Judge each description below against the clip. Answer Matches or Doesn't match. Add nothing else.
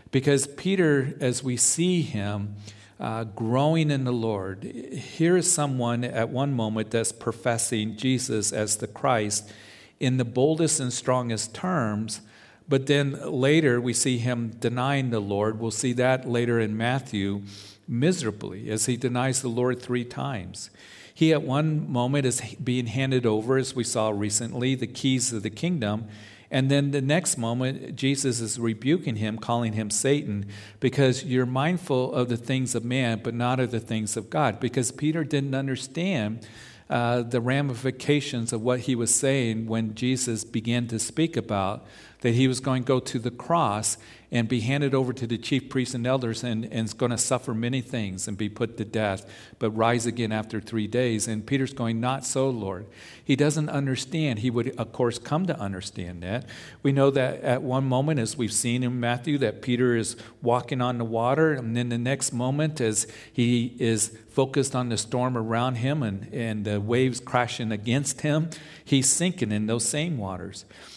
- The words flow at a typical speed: Matches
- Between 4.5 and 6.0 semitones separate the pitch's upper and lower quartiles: Doesn't match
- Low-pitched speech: Matches